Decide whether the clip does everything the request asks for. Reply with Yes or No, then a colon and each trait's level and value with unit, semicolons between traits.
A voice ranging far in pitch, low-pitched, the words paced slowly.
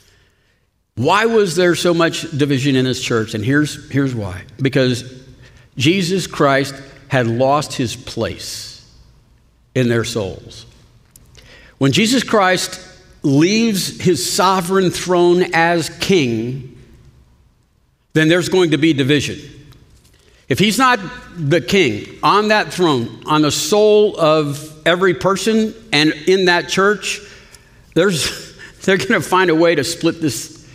No: wide, 6.4 semitones; medium, 155 Hz; slow, 130 wpm